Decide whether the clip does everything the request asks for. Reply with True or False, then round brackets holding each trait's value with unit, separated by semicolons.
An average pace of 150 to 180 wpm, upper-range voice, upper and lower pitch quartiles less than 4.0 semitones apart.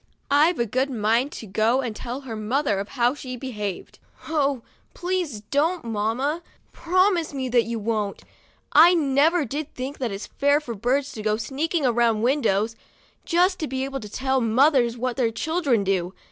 False (175 wpm; 255 Hz; 4.4 semitones)